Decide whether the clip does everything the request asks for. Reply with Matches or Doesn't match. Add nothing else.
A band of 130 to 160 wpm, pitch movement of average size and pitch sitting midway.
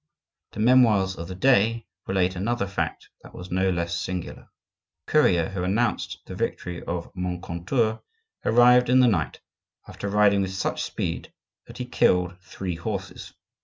Doesn't match